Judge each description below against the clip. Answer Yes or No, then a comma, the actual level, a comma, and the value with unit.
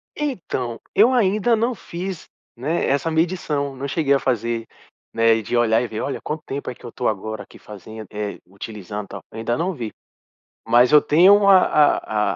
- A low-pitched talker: Yes, low, 130 Hz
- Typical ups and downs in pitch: No, wide, 7.3 semitones